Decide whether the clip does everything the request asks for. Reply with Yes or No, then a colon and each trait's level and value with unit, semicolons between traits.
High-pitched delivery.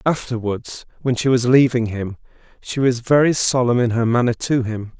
No: low, 120 Hz